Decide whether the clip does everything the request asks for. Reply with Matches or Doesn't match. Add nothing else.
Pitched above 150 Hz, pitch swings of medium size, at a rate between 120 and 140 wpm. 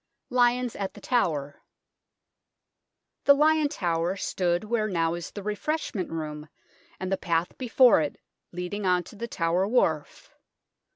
Doesn't match